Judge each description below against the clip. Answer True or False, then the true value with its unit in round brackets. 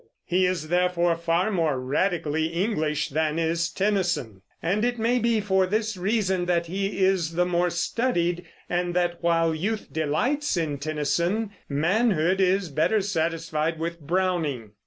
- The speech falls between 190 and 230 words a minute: False (145 wpm)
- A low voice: False (175 Hz)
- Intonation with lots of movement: False (3.1 semitones)